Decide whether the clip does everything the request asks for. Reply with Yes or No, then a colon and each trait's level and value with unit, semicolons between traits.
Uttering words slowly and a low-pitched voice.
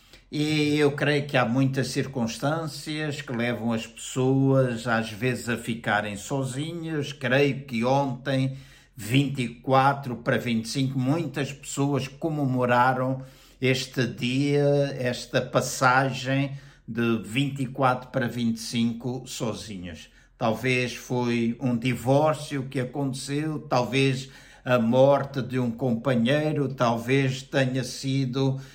Yes: slow, 100 wpm; low, 130 Hz